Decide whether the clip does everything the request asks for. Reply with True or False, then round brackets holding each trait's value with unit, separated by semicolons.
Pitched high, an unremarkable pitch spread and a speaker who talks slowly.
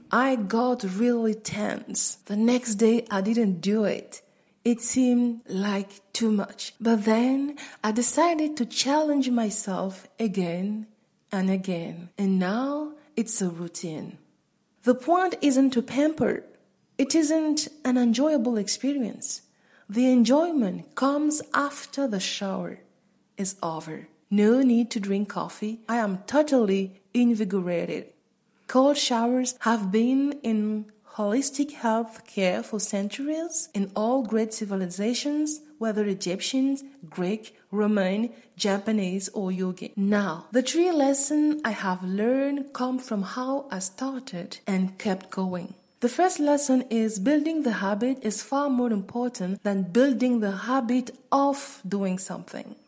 True (230 Hz; 5.0 semitones; 125 wpm)